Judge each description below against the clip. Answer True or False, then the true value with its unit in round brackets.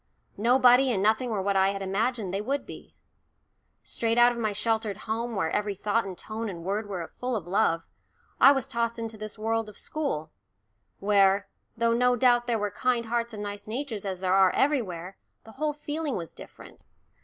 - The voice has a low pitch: False (220 Hz)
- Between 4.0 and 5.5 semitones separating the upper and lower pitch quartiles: False (3.4 semitones)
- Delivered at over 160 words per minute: True (195 wpm)